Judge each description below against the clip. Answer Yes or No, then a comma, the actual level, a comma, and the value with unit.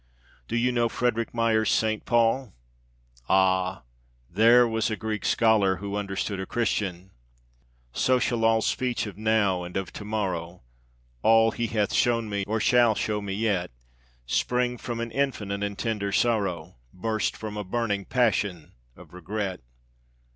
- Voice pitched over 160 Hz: No, low, 110 Hz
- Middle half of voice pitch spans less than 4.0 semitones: Yes, average, 3.0 semitones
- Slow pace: No, average, 150 wpm